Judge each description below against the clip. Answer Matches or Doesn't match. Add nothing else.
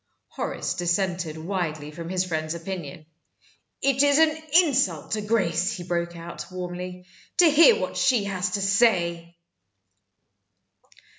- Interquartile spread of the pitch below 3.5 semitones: Doesn't match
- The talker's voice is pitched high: Doesn't match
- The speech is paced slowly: Matches